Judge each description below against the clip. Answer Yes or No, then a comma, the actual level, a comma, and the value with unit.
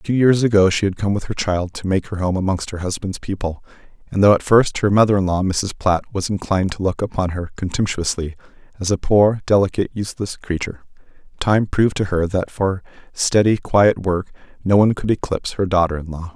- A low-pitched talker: Yes, very low, 95 Hz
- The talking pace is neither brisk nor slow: No, fast, 210 wpm